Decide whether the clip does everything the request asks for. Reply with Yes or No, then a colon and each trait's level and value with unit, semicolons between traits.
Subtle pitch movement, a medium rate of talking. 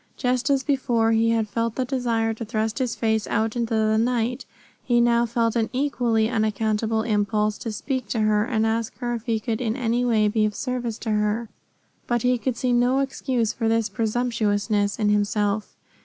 Yes: narrow, 2.0 semitones; average, 195 wpm